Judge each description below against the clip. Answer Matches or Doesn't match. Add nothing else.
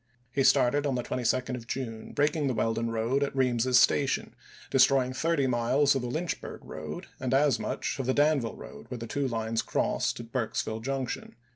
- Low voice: Matches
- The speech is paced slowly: Doesn't match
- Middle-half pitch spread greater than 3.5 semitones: Doesn't match